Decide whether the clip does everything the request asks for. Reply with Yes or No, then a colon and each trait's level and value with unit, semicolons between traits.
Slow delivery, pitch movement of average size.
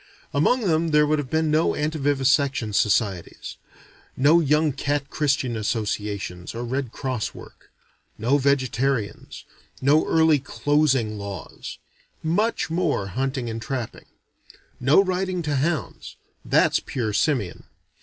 Yes: slow, 120 wpm; average, 4.9 semitones